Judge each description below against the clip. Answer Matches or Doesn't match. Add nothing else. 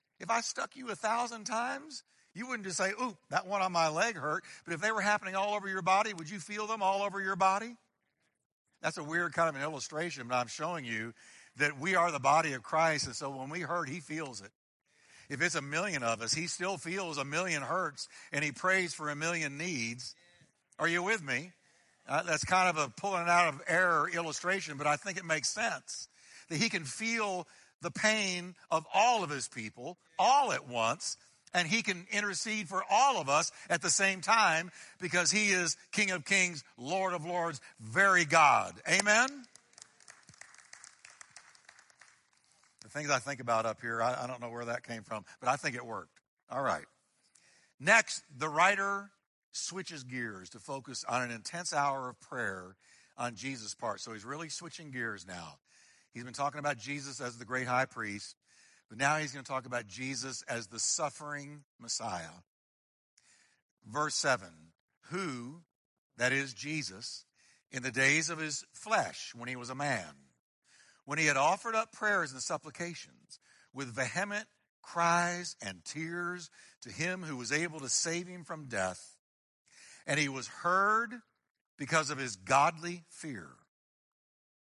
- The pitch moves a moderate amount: Doesn't match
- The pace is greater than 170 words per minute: Matches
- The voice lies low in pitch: Doesn't match